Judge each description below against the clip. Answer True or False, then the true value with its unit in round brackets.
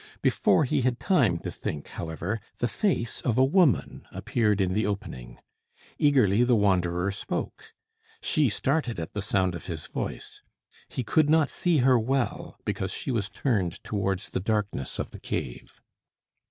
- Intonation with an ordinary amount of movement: False (5.8 semitones)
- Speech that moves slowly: False (160 wpm)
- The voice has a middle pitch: False (110 Hz)